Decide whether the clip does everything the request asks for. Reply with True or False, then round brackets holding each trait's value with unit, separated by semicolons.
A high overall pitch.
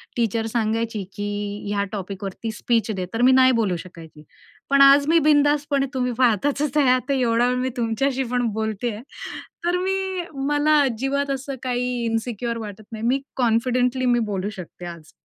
True (245 Hz)